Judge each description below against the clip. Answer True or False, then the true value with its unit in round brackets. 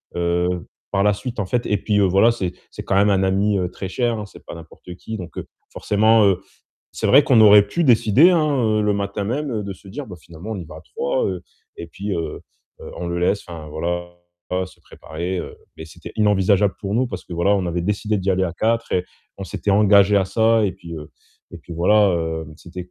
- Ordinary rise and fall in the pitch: True (3.3 semitones)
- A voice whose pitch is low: True (100 Hz)